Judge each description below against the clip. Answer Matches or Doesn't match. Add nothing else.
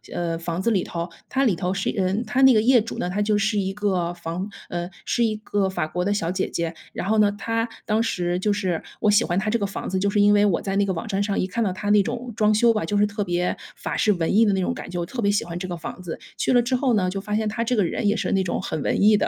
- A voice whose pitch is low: Doesn't match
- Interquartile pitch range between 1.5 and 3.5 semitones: Matches